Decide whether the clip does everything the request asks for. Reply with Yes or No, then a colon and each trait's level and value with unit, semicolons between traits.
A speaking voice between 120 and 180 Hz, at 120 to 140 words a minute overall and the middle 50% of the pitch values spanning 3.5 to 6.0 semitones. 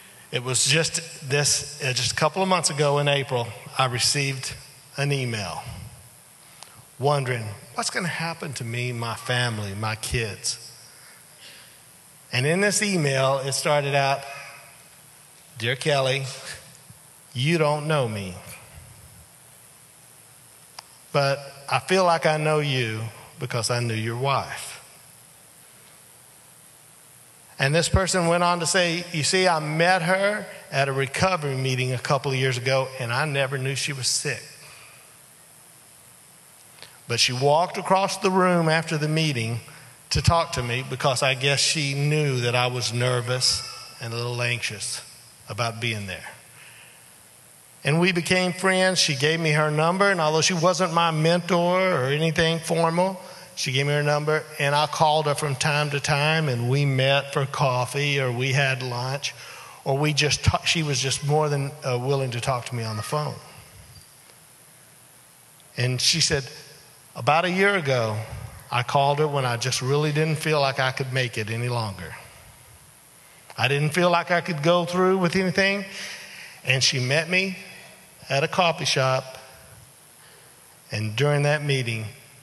No: medium, 140 Hz; average, 155 wpm; average, 4.0 semitones